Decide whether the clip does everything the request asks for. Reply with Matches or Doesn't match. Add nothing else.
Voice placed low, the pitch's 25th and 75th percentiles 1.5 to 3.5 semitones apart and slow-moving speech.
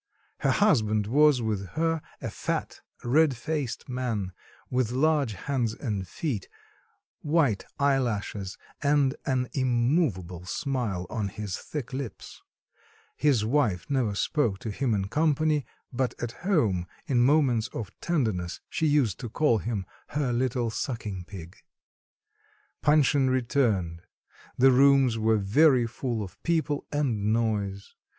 Doesn't match